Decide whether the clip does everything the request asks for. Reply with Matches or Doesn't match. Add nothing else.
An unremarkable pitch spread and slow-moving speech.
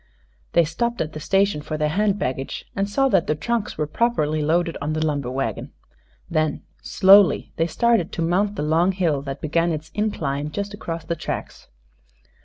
Doesn't match